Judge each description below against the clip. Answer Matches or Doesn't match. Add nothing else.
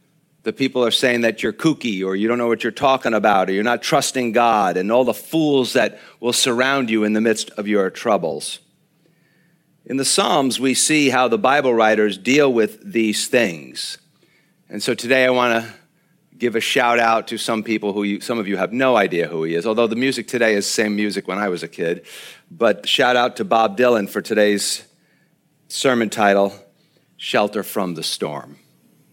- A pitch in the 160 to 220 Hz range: Doesn't match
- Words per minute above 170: Matches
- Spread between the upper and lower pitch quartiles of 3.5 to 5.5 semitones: Matches